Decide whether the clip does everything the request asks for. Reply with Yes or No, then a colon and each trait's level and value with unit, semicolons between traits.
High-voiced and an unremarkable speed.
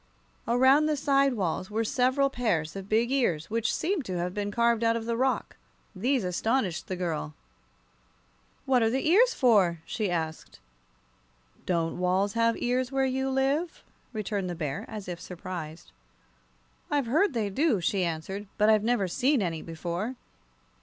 Yes: high, 220 Hz; average, 165 wpm